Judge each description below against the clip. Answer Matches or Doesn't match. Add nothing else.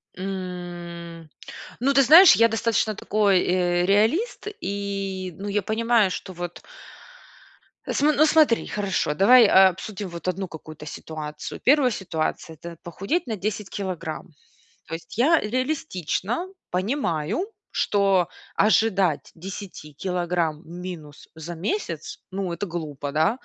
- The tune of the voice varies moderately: Matches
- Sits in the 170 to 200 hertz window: Matches